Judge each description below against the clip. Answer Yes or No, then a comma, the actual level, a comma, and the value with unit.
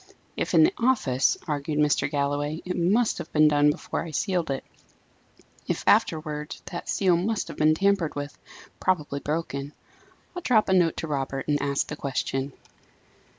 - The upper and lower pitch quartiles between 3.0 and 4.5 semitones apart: Yes, average, 4.0 semitones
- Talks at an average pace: Yes, average, 165 wpm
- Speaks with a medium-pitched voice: Yes, medium, 155 Hz